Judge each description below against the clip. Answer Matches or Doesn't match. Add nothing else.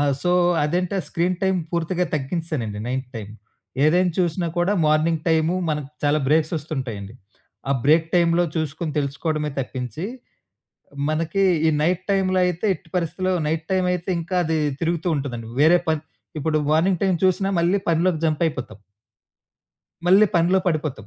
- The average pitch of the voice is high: Doesn't match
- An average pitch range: Matches